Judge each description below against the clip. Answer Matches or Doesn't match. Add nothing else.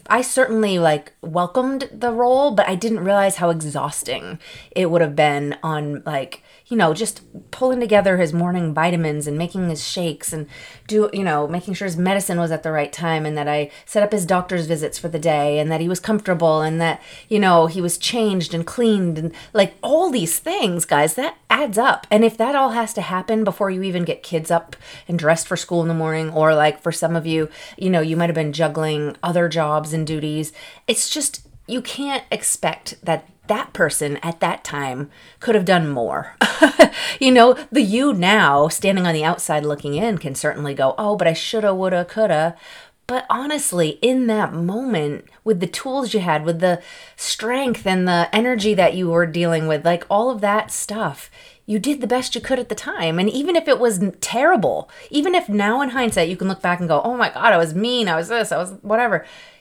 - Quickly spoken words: Matches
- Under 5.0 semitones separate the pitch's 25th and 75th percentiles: Doesn't match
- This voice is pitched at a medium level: Matches